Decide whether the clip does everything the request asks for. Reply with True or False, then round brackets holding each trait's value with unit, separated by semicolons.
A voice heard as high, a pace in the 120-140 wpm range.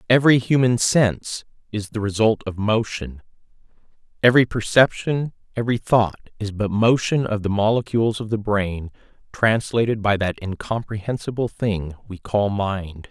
False (110 Hz; 135 wpm)